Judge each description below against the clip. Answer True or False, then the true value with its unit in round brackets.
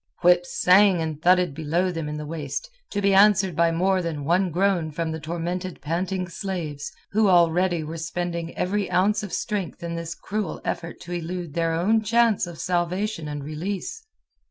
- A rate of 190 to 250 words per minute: False (180 wpm)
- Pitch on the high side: False (175 Hz)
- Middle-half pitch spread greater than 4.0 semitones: False (2.6 semitones)